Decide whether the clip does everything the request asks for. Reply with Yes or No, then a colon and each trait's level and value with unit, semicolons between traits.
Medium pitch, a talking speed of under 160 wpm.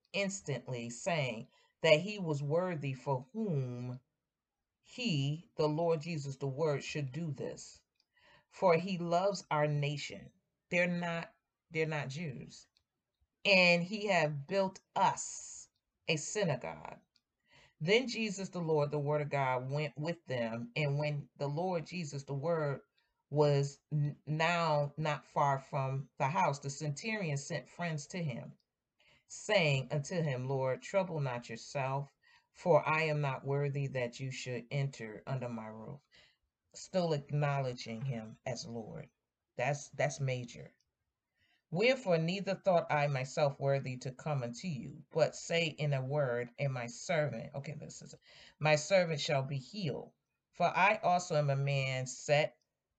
Yes: medium, 150 Hz; average, 140 wpm